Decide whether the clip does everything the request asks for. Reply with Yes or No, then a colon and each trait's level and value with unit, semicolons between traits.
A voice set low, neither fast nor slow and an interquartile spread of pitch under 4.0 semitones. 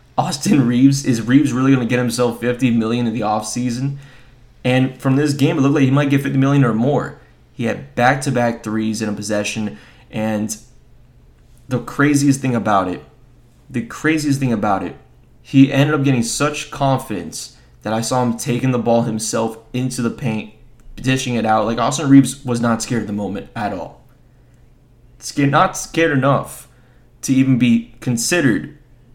Yes: low, 125 Hz; average, 175 wpm; average, 2.9 semitones